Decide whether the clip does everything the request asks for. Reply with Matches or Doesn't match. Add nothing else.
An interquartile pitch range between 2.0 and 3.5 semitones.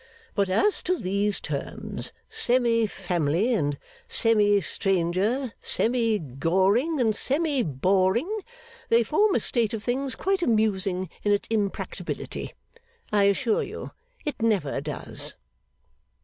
Doesn't match